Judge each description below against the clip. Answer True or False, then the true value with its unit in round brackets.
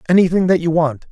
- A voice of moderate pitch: True (170 Hz)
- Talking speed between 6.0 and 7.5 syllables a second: True (6.5 syllables/s)